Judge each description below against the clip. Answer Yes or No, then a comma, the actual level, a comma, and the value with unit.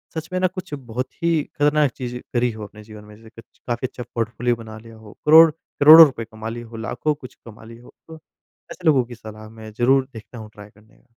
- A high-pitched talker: No, low, 120 Hz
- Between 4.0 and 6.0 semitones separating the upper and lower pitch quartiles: Yes, average, 4.7 semitones